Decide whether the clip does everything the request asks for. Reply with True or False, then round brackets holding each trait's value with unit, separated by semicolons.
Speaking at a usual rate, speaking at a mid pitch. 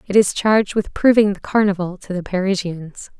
False (190 wpm; 195 Hz)